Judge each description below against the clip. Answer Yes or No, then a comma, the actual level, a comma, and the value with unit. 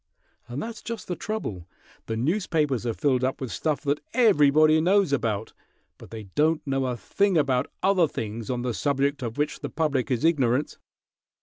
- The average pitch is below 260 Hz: Yes, medium, 140 Hz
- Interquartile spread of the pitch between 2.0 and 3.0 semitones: No, average, 4.7 semitones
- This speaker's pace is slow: No, average, 180 wpm